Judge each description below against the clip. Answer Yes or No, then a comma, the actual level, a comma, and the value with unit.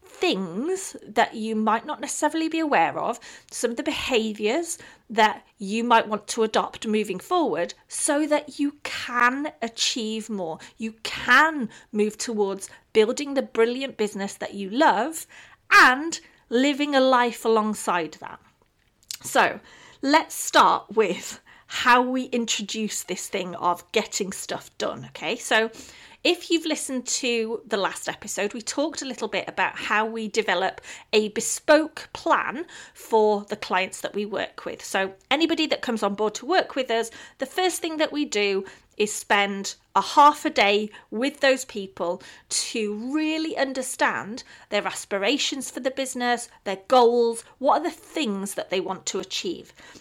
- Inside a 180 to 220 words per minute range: No, average, 155 wpm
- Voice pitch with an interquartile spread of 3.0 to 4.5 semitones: No, wide, 5.5 semitones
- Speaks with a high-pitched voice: Yes, high, 230 Hz